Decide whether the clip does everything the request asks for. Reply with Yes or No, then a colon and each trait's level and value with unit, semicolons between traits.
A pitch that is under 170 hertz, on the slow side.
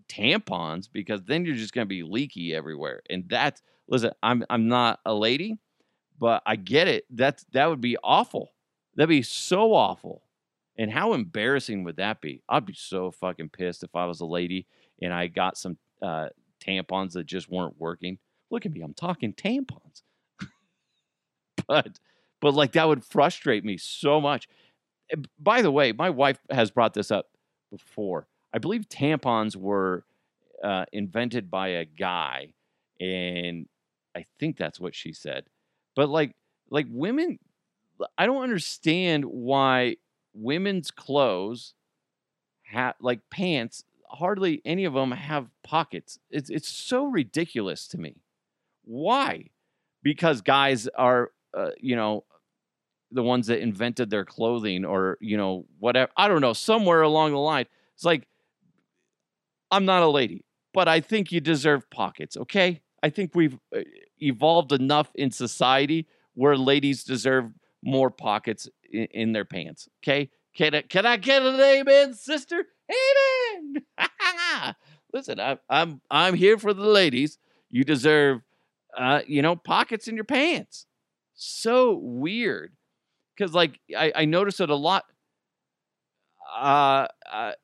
No: medium, 140 Hz; average, 145 wpm